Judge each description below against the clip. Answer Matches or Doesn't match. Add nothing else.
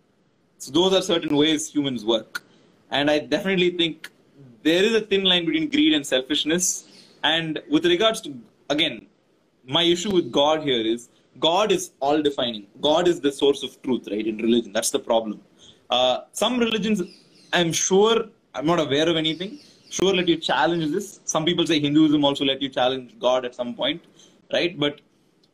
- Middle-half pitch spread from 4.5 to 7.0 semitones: Matches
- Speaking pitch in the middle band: Matches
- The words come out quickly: Matches